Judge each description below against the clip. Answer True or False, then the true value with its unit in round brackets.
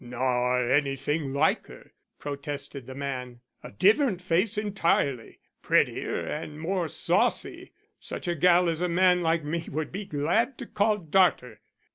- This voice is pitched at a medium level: True (155 Hz)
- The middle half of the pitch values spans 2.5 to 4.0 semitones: False (4.8 semitones)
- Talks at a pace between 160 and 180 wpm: False (145 wpm)